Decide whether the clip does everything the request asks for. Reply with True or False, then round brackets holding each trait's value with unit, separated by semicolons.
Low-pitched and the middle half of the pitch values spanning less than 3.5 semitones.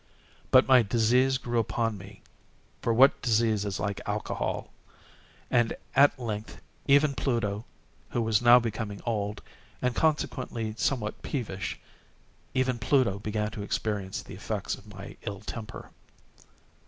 True (115 Hz; 3.1 semitones)